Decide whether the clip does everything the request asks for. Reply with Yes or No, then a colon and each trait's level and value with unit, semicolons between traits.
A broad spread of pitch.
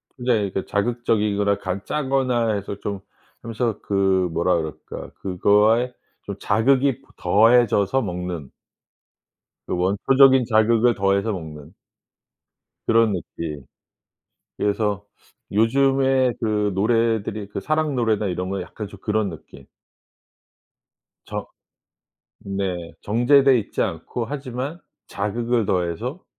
No: average, 3.8 semitones